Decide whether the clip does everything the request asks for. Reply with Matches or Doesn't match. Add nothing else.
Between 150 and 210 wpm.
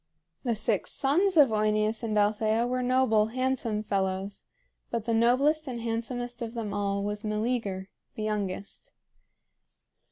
Doesn't match